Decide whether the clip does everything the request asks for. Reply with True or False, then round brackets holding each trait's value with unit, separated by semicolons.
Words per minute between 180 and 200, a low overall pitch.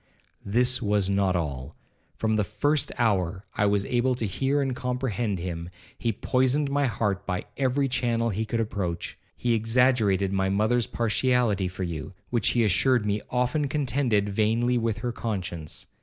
False (160 wpm; 110 Hz)